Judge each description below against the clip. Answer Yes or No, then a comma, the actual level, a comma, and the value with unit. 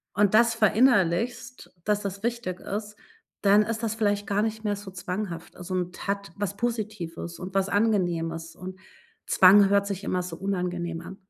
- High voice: Yes, high, 200 Hz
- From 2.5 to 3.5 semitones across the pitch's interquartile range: Yes, average, 2.8 semitones